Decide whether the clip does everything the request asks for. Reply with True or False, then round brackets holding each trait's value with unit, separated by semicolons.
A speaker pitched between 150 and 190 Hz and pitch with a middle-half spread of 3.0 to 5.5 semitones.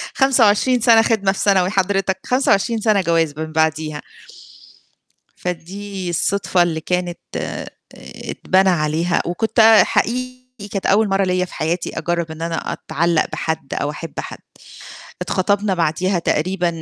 True (185 Hz; 3.5 semitones)